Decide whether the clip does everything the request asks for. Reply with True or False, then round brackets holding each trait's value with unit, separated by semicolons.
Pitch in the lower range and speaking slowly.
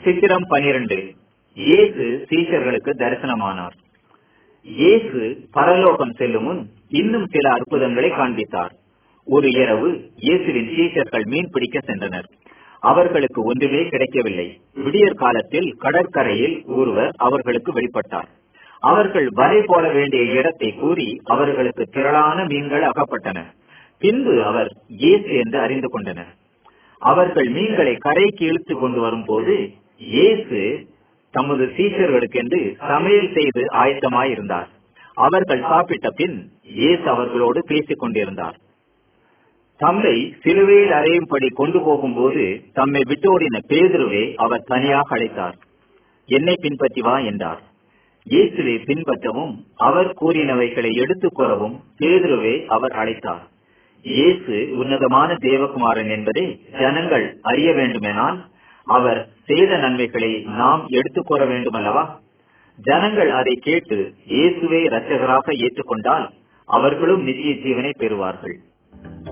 False (145 Hz; 90 wpm)